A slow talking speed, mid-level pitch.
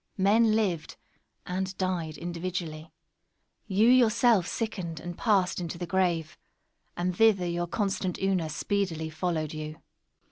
Yes: slow, 120 wpm; medium, 180 Hz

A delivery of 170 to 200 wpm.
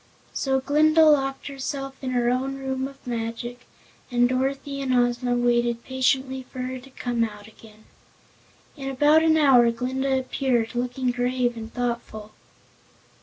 No: average, 145 wpm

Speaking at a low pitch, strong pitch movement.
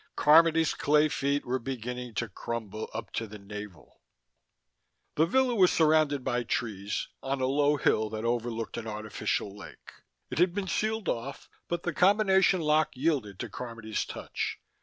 Yes: low, 130 Hz; wide, 6.3 semitones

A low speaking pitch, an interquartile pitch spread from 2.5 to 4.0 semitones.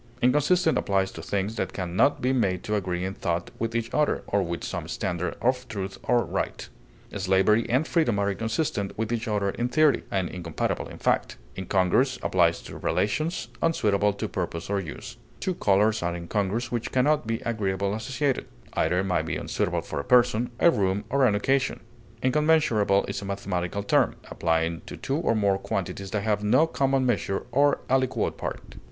No: low, 105 Hz; average, 4.9 semitones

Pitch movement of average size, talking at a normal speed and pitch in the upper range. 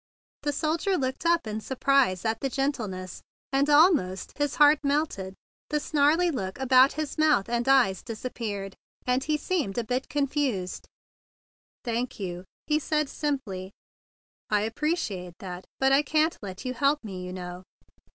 No: wide, 6.9 semitones; average, 155 wpm; very high, 260 Hz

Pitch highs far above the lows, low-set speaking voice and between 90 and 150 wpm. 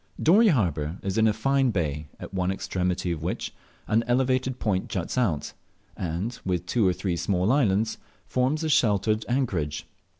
No: wide, 5.9 semitones; low, 100 Hz; average, 165 wpm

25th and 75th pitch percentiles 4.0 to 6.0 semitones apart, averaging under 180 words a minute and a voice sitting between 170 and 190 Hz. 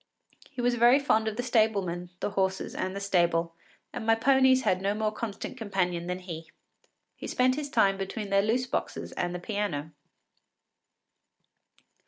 No: average, 4.6 semitones; average, 165 wpm; high, 205 Hz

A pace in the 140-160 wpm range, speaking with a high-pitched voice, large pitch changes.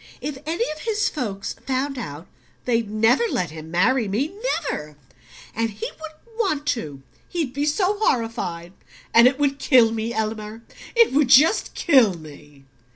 Yes: average, 155 wpm; high, 245 Hz; wide, 6.7 semitones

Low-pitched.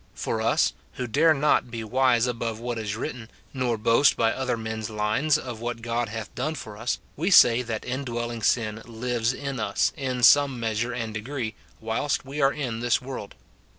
Yes: low, 120 Hz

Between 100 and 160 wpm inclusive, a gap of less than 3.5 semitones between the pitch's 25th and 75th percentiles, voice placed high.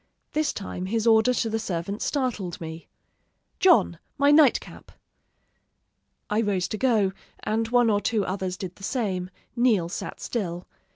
No: average, 155 wpm; average, 4.6 semitones; high, 215 Hz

